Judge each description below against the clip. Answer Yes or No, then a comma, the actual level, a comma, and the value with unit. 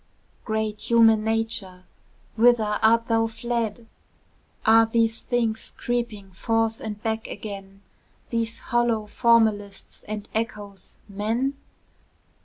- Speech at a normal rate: No, slow, 100 wpm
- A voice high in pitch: Yes, high, 225 Hz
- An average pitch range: No, narrow, 1.6 semitones